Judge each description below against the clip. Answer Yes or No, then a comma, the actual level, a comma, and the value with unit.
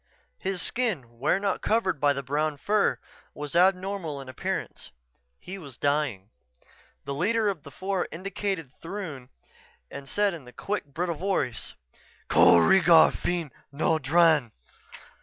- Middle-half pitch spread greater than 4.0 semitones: Yes, wide, 5.5 semitones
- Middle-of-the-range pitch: Yes, medium, 165 Hz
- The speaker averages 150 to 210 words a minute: No, average, 140 wpm